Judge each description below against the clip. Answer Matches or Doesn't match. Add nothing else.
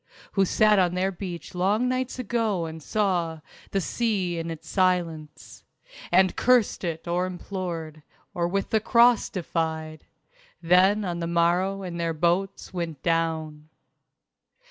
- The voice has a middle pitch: Matches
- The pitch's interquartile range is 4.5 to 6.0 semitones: Doesn't match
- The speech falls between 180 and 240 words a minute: Doesn't match